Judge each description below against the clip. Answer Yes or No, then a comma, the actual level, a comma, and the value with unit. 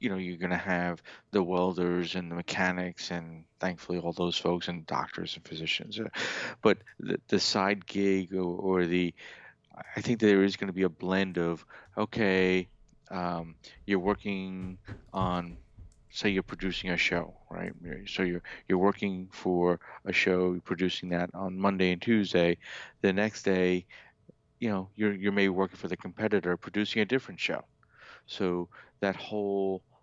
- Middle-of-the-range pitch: No, very low, 95 Hz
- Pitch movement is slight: Yes, narrow, 1.8 semitones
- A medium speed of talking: Yes, average, 165 wpm